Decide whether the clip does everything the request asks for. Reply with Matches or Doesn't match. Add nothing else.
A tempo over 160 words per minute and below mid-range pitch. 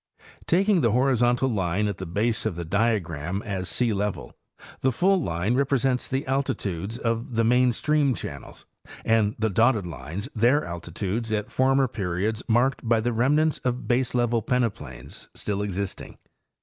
Doesn't match